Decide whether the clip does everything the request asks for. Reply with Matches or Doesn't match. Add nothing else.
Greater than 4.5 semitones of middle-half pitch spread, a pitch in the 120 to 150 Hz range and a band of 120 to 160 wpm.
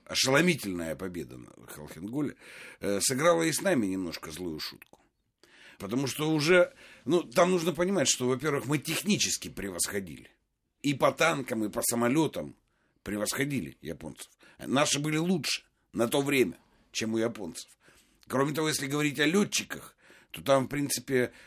Matches